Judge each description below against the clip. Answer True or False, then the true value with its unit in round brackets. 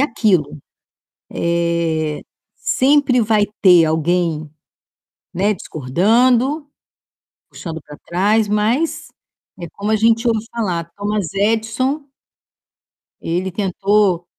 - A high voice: True (205 Hz)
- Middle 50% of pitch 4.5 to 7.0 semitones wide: True (5.0 semitones)